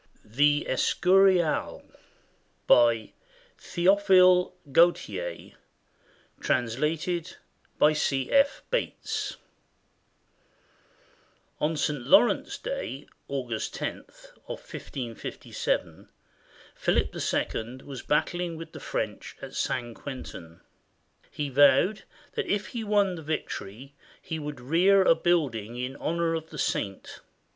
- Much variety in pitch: Yes, wide, 5.8 semitones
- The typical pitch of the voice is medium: Yes, medium, 160 Hz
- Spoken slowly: Yes, slow, 100 wpm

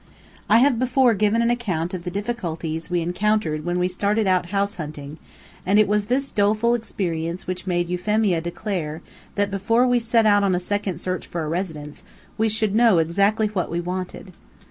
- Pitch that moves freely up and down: No, average, 3.8 semitones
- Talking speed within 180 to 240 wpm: Yes, average, 190 wpm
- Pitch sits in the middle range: No, high, 195 Hz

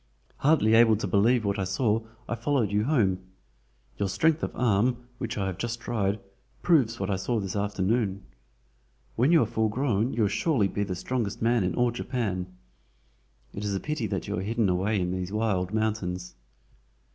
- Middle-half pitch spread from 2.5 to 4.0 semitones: Yes, average, 3.5 semitones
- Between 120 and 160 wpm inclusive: No, average, 190 wpm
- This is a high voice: No, low, 110 Hz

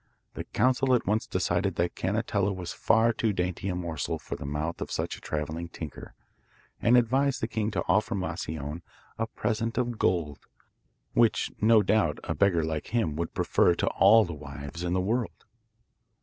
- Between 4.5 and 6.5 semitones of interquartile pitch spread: Yes, average, 5.1 semitones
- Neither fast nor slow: Yes, average, 180 wpm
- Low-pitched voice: Yes, very low, 95 Hz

